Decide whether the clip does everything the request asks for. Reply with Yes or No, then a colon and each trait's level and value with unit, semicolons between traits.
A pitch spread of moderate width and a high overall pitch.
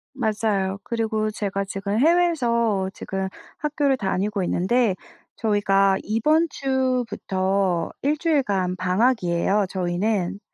Yes: average, 4.7 semitones; high, 210 Hz